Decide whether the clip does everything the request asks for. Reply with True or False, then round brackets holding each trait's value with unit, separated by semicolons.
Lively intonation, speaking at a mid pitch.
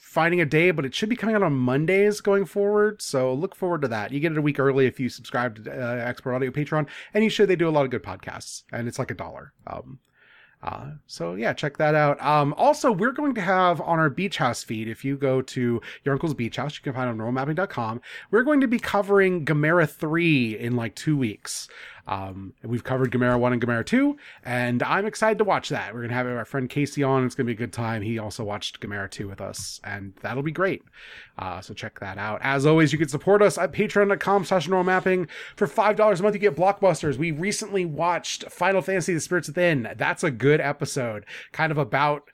True (7.3 semitones; 145 Hz)